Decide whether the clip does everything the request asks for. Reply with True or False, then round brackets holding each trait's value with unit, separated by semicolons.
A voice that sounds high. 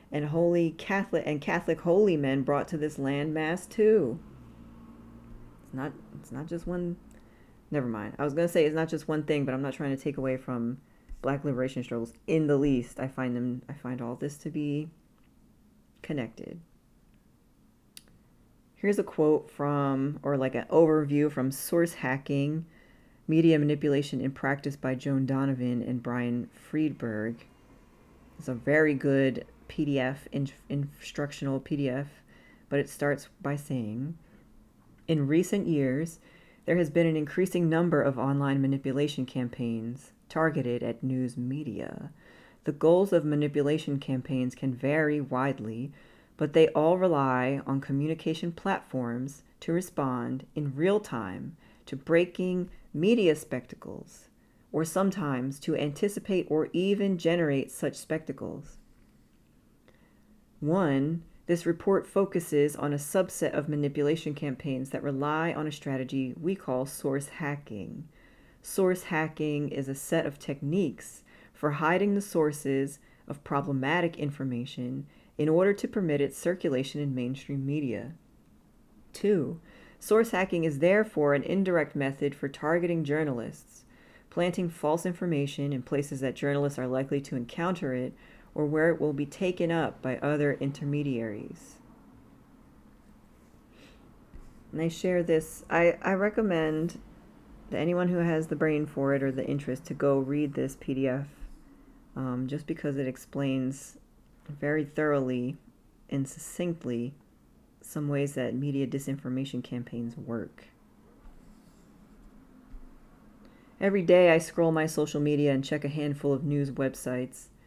False (145 Hz)